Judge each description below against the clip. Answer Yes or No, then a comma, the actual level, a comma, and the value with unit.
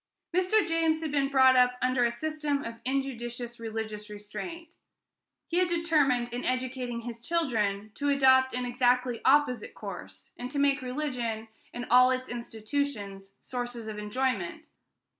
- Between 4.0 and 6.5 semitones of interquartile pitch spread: No, average, 3.3 semitones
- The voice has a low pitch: No, very high, 255 Hz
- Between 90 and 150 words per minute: Yes, average, 145 wpm